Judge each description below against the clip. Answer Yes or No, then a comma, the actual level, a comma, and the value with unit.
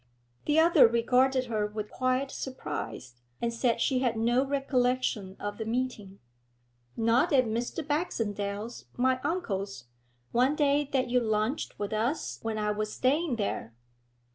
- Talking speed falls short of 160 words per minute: Yes, average, 140 wpm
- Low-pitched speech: No, high, 240 Hz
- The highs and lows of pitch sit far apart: No, average, 3.8 semitones